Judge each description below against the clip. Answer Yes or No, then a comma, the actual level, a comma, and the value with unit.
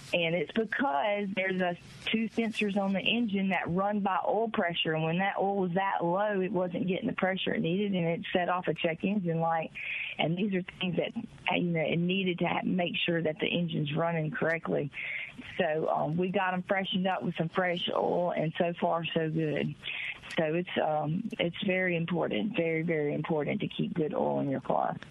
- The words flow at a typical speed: No, fast, 210 wpm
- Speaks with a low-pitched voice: No, medium, 180 Hz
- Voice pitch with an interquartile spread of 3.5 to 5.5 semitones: No, average, 3.0 semitones